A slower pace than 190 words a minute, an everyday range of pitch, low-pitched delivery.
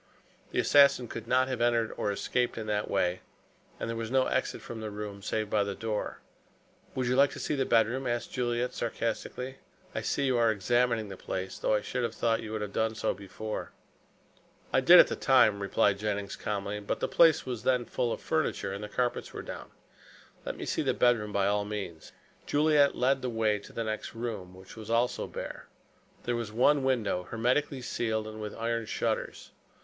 No: fast, 205 wpm; average, 3.0 semitones; low, 115 Hz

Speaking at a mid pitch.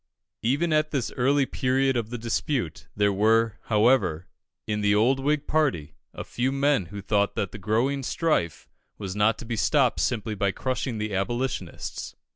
No: low, 115 Hz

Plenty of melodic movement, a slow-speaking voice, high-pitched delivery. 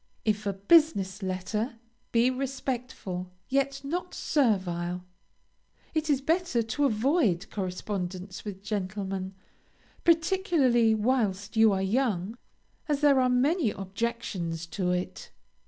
Yes: wide, 6.1 semitones; slow, 110 wpm; high, 220 Hz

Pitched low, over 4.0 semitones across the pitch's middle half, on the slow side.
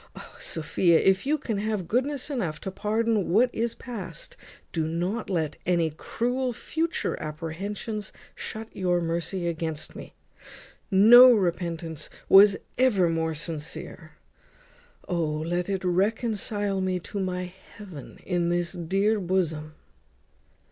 No: medium, 185 Hz; average, 4.4 semitones; slow, 125 wpm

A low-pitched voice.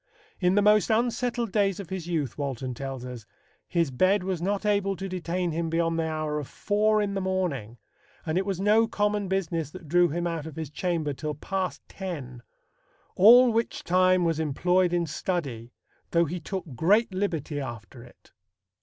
No: medium, 175 Hz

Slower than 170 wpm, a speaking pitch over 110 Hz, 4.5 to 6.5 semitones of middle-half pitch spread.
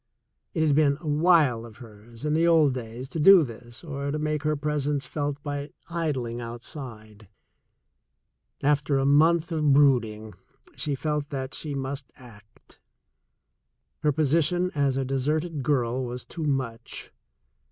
No: average, 150 wpm; medium, 140 Hz; average, 3.6 semitones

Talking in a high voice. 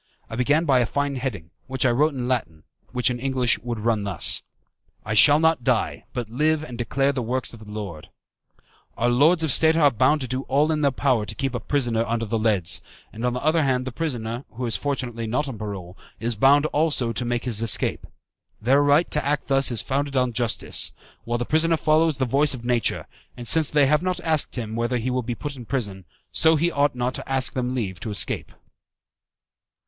No: low, 125 Hz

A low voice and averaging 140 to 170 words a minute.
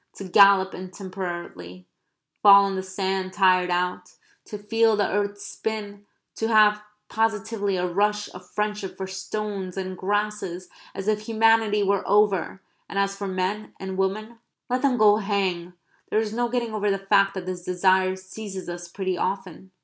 No: high, 195 Hz; average, 165 wpm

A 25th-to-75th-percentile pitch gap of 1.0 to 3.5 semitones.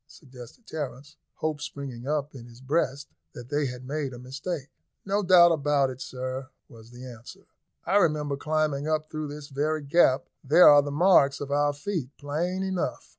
Yes: average, 3.0 semitones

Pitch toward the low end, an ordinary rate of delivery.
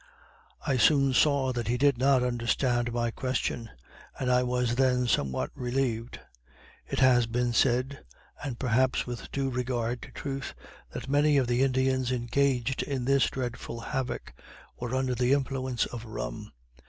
Yes: low, 125 Hz; average, 155 wpm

